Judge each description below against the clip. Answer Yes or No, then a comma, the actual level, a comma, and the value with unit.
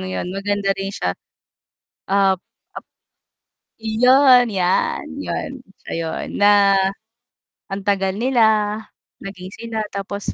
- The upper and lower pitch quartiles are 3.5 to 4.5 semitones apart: No, narrow, 2.5 semitones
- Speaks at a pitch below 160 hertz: No, high, 200 Hz